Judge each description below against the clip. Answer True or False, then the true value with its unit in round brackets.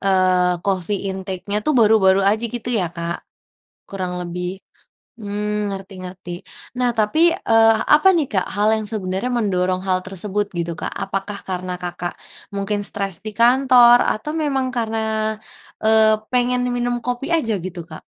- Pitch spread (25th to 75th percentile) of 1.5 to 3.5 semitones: False (4.0 semitones)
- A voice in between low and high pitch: False (205 Hz)